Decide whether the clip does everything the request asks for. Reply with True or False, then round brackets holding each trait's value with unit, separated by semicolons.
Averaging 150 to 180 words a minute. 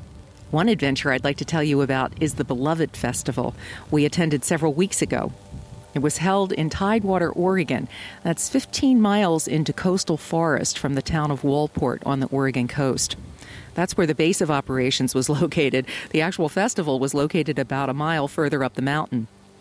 True (175 wpm)